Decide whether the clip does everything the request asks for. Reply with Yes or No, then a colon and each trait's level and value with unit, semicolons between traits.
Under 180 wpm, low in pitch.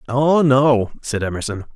Yes: slow, 135 wpm; low, 125 Hz